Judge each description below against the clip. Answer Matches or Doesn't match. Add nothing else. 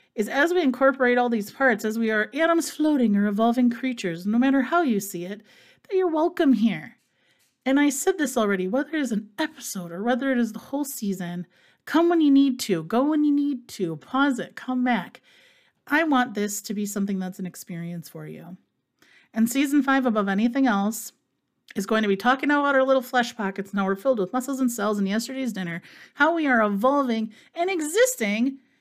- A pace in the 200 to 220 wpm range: Matches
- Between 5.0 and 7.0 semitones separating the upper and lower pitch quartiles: Matches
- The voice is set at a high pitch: Matches